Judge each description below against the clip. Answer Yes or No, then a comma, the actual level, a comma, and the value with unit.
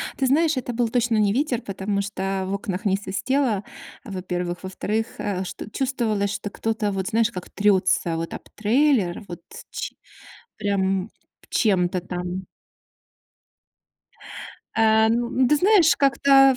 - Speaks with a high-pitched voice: Yes, high, 210 Hz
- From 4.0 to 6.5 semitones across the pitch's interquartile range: Yes, average, 4.3 semitones